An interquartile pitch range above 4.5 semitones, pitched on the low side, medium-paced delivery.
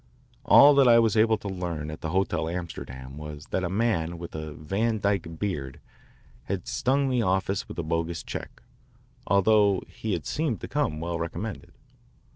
Yes: average, 5.2 semitones; very low, 90 Hz; average, 175 wpm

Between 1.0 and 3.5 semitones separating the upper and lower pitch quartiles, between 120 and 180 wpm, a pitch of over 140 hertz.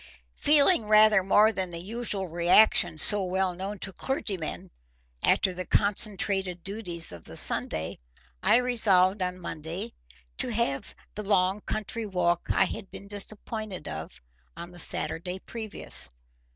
Yes: average, 3.2 semitones; average, 140 wpm; high, 190 Hz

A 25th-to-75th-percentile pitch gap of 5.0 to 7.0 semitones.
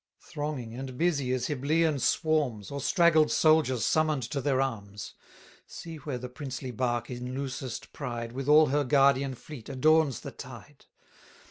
No: average, 3.3 semitones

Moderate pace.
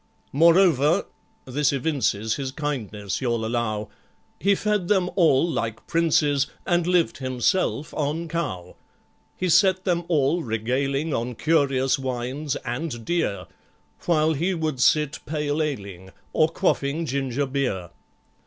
No: slow, 125 wpm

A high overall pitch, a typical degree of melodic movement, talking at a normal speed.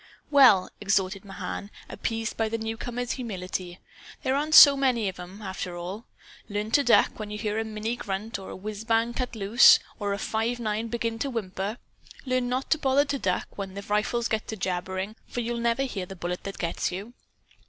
Yes: high, 220 Hz; average, 3.5 semitones; average, 195 wpm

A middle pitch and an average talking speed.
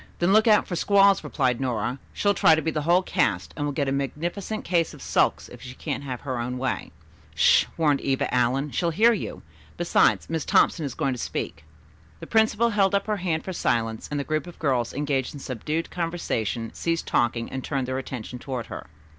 No: medium, 145 Hz; fast, 220 wpm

